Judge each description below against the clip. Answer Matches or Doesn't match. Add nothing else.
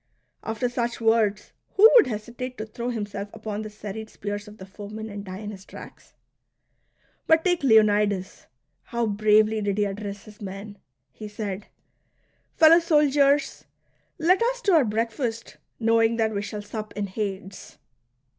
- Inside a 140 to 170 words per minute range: Matches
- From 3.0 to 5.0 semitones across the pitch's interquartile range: Doesn't match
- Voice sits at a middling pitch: Doesn't match